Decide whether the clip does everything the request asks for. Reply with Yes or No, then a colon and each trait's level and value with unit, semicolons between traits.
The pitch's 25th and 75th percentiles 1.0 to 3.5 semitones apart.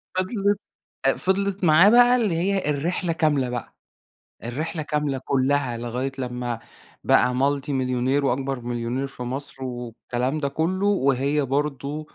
No: average, 4.4 semitones